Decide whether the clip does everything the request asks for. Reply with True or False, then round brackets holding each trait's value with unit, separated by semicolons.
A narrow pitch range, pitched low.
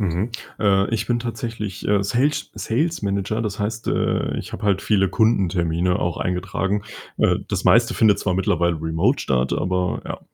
False (3.7 semitones; 100 Hz)